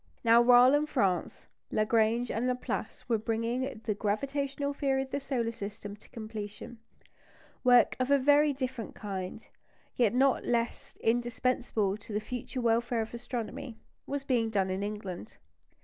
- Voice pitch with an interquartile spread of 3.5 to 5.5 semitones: No, average, 3.1 semitones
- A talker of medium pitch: No, high, 235 Hz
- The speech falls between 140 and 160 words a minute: Yes, average, 150 wpm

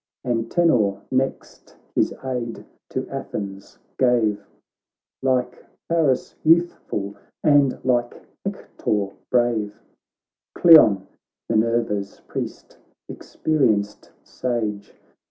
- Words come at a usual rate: No, slow, 75 wpm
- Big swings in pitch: No, average, 4.1 semitones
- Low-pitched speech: Yes, low, 120 Hz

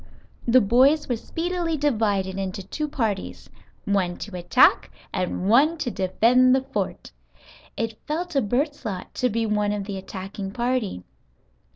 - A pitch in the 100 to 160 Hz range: No, high, 225 Hz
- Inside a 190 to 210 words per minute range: No, average, 150 wpm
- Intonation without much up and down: No, average, 5.3 semitones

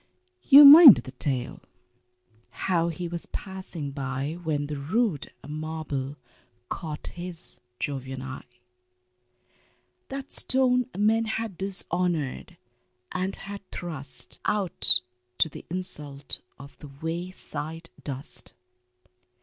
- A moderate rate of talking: No, slow, 100 wpm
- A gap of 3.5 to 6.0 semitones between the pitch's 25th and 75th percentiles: Yes, average, 5.2 semitones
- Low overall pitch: No, medium, 165 Hz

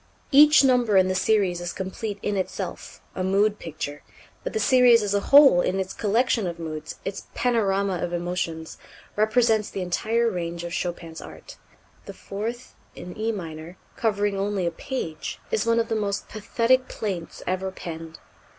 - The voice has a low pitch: No, high, 200 Hz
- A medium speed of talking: Yes, average, 170 wpm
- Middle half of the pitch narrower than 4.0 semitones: No, average, 4.5 semitones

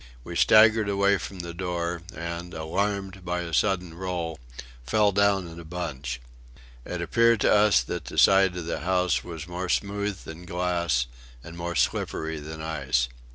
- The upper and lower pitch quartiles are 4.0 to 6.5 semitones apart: No, average, 2.9 semitones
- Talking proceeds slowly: No, average, 165 wpm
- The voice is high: No, very low, 90 Hz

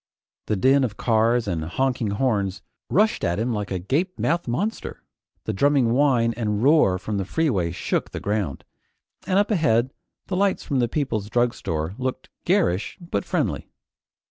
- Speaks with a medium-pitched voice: No, low, 120 Hz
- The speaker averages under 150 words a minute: No, average, 165 wpm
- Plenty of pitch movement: Yes, wide, 5.8 semitones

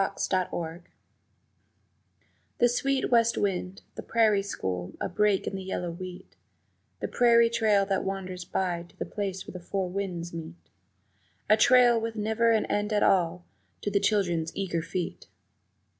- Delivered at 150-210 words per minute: Yes, average, 160 wpm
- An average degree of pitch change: Yes, average, 3.6 semitones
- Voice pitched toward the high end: Yes, high, 195 Hz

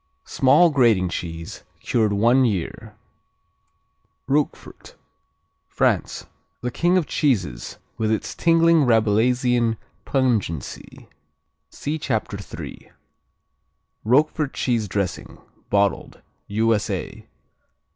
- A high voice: No, low, 115 Hz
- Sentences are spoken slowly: Yes, slow, 80 wpm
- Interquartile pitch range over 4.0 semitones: Yes, average, 5.1 semitones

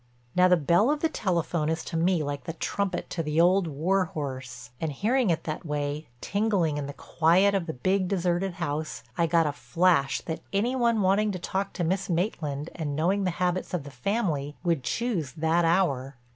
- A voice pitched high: No, medium, 170 Hz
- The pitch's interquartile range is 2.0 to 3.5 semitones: No, average, 4.2 semitones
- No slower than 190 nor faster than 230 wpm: Yes, average, 200 wpm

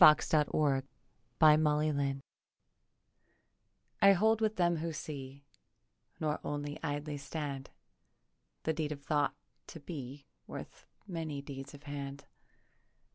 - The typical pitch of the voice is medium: Yes, medium, 150 Hz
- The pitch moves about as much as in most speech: No, narrow, 2.1 semitones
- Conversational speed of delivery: No, slow, 105 wpm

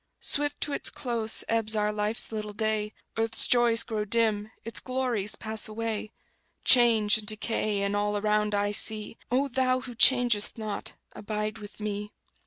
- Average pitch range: No, narrow, 1.8 semitones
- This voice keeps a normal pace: Yes, average, 160 wpm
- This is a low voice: No, high, 215 Hz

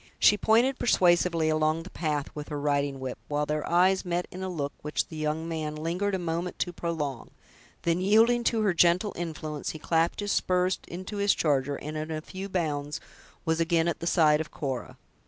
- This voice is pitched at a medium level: Yes, medium, 165 Hz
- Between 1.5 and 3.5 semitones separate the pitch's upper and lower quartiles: Yes, average, 3.2 semitones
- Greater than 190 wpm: Yes, average, 200 wpm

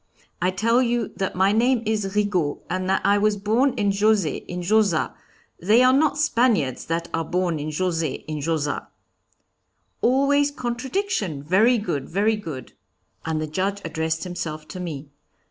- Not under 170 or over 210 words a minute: No, average, 160 wpm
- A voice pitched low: No, high, 195 Hz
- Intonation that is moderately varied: No, wide, 5.9 semitones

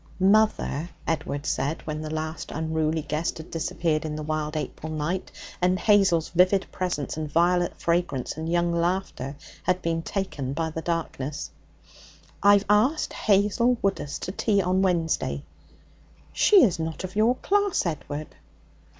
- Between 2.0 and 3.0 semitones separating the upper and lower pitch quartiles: No, average, 3.6 semitones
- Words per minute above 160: No, average, 145 wpm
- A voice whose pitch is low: No, medium, 170 Hz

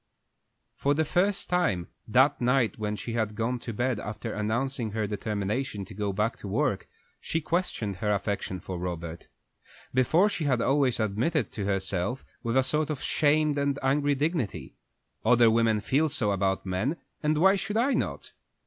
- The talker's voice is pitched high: No, low, 120 Hz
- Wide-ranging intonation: Yes, wide, 5.7 semitones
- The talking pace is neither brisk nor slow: Yes, average, 175 wpm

